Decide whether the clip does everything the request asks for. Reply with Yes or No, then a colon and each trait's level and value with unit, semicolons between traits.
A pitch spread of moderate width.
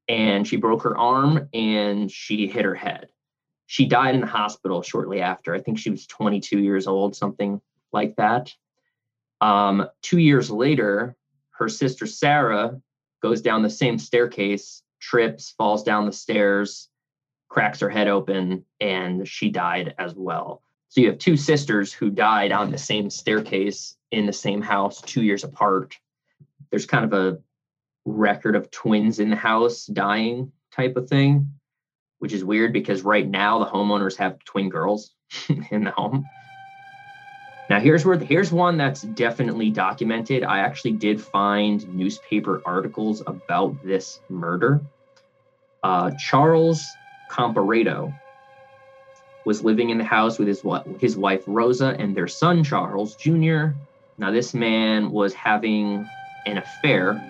No: wide, 5.9 semitones